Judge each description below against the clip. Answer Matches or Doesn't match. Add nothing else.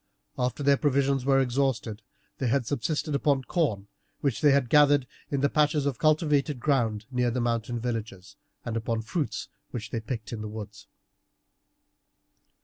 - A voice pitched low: Matches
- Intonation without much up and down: Doesn't match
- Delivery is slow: Doesn't match